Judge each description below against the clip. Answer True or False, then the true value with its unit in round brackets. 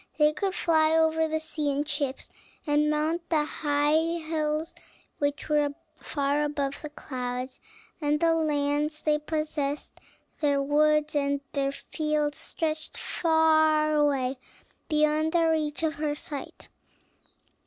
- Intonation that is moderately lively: False (1.4 semitones)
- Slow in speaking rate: True (130 wpm)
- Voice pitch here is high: True (300 Hz)